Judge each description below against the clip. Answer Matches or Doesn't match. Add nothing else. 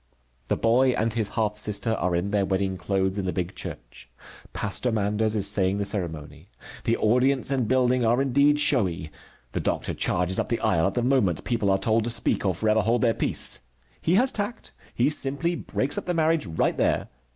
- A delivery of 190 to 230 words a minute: Matches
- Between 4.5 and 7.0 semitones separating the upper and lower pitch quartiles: Matches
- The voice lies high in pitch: Doesn't match